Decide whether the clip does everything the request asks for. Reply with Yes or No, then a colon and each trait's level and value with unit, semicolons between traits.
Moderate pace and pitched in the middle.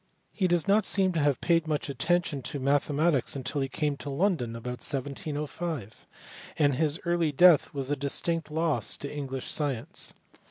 Yes: average, 165 wpm; medium, 145 Hz